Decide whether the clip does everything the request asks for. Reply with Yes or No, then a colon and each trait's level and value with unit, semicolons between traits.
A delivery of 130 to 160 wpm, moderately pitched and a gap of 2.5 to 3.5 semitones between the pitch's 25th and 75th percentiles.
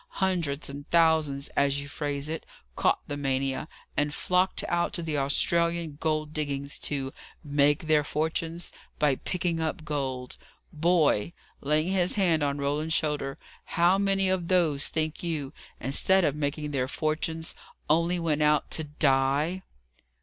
Yes: average, 145 wpm; medium, 155 Hz; average, 2.9 semitones